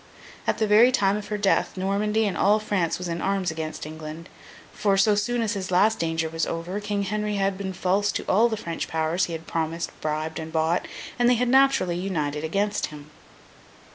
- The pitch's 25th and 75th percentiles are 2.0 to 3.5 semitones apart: No, average, 4.3 semitones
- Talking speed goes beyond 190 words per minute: Yes, fast, 205 wpm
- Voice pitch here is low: No, high, 190 Hz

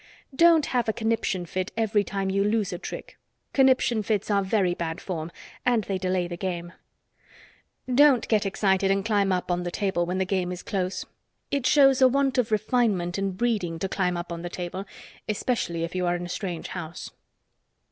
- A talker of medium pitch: No, high, 195 Hz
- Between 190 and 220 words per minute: Yes, average, 195 wpm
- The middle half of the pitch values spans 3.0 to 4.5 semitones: Yes, average, 3.9 semitones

